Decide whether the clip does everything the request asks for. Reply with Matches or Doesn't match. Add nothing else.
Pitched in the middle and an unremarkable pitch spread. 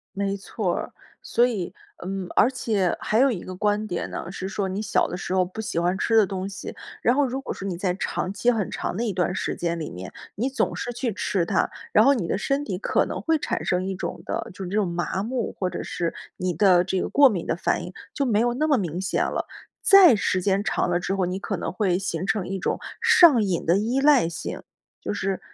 Doesn't match